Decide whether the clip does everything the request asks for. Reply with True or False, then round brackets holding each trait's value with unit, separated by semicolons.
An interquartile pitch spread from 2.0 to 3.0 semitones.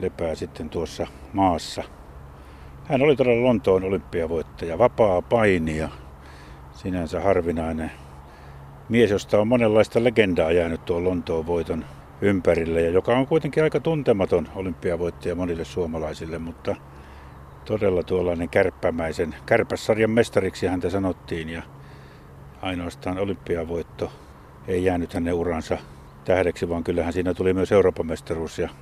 False (5.0 semitones)